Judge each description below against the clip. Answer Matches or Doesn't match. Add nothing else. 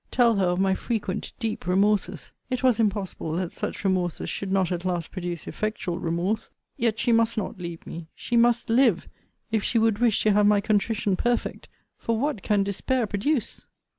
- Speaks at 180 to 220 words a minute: Matches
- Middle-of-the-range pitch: Doesn't match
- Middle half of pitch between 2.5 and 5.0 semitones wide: Matches